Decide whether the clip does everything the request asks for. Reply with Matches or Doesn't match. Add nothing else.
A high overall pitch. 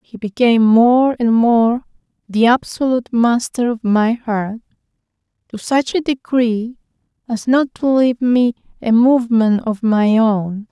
Matches